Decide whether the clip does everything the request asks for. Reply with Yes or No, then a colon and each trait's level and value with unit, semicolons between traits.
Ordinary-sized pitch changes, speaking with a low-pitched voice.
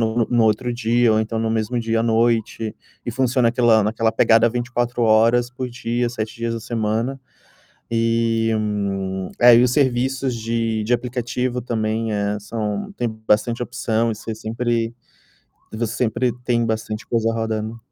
No: narrow, 1.5 semitones; low, 115 Hz